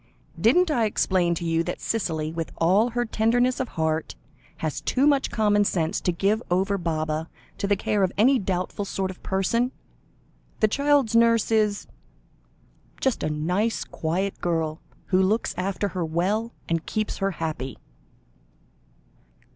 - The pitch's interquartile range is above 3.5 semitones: Yes, average, 5.1 semitones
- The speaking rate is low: No, average, 150 wpm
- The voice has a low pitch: No, high, 195 Hz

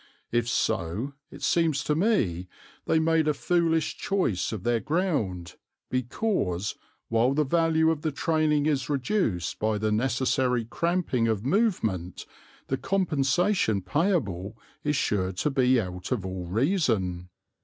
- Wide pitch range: Yes, wide, 7.6 semitones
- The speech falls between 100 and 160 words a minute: Yes, slow, 135 wpm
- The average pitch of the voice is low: Yes, low, 130 Hz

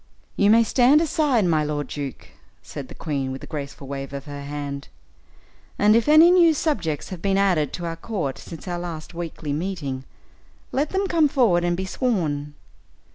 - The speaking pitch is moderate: Yes, medium, 175 Hz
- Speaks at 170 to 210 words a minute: Yes, average, 185 wpm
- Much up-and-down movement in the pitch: Yes, wide, 7.9 semitones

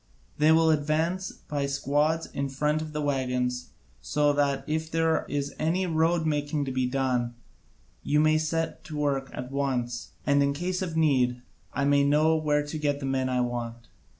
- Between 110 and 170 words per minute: No, average, 180 wpm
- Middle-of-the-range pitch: Yes, medium, 145 Hz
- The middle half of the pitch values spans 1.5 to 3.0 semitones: Yes, narrow, 2.6 semitones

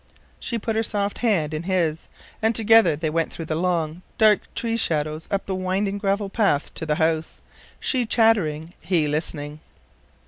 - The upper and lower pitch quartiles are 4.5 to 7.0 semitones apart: Yes, average, 5.2 semitones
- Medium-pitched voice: Yes, medium, 180 Hz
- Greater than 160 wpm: Yes, average, 170 wpm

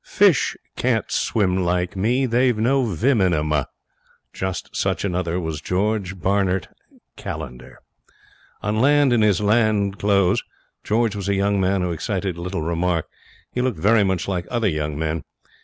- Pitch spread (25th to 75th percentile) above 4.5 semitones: No, average, 3.6 semitones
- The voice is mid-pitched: No, very low, 95 Hz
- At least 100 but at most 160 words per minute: Yes, average, 155 wpm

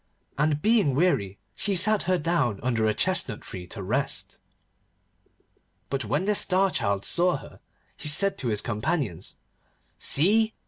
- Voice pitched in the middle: Yes, medium, 145 Hz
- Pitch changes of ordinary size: No, wide, 9.0 semitones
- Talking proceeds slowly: No, average, 145 wpm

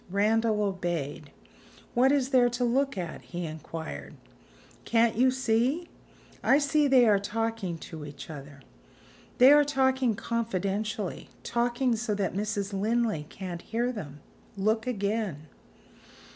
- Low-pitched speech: No, high, 220 Hz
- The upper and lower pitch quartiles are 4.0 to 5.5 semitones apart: Yes, average, 5.0 semitones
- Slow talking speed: Yes, slow, 130 wpm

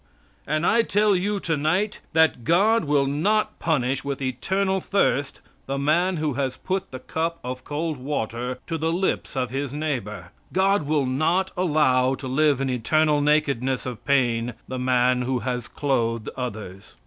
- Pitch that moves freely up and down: No, average, 4.5 semitones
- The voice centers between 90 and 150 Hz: Yes, medium, 140 Hz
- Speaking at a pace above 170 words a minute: No, average, 160 wpm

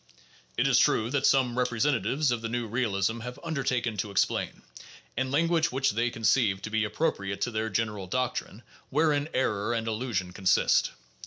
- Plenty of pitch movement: No, average, 3.6 semitones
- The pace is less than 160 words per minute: No, average, 175 wpm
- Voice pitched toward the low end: Yes, low, 120 Hz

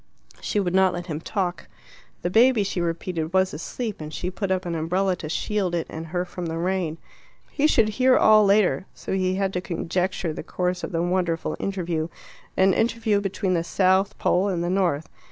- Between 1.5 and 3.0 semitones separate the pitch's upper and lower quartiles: Yes, narrow, 2.4 semitones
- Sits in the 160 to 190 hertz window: Yes, medium, 185 Hz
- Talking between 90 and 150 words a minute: No, average, 200 wpm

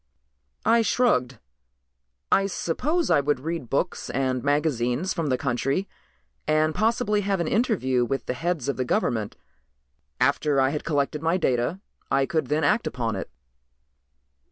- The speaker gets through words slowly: No, average, 150 wpm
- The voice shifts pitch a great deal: Yes, wide, 6.3 semitones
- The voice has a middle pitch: Yes, medium, 150 Hz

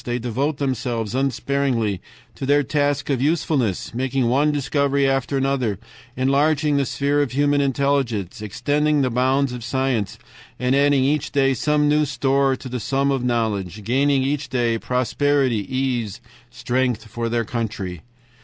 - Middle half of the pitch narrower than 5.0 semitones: Yes, average, 2.9 semitones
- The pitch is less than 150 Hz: Yes, low, 135 Hz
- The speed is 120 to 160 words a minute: Yes, average, 145 wpm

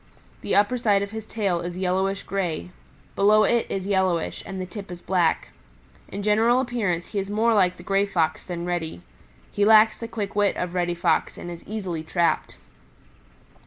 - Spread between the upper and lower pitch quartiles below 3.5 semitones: Yes, average, 3.1 semitones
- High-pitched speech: Yes, high, 195 Hz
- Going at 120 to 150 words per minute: No, average, 185 wpm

